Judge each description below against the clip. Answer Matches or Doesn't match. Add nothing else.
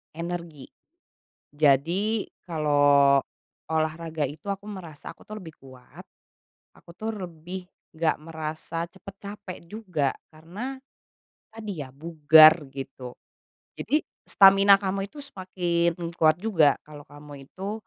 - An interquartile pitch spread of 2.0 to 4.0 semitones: Doesn't match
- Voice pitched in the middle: Matches